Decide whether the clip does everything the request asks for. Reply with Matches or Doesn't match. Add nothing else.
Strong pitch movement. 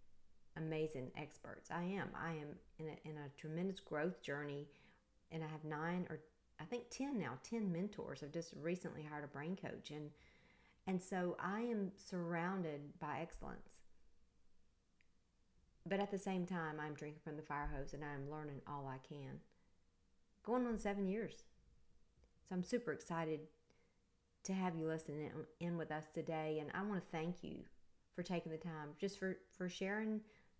Doesn't match